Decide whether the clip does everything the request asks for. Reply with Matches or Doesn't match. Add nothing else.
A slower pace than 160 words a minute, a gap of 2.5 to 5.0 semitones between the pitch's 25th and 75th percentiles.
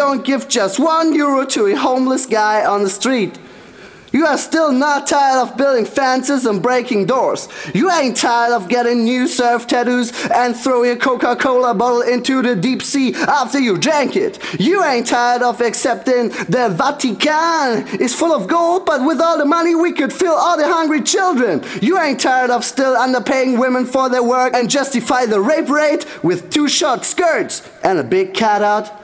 Doesn't match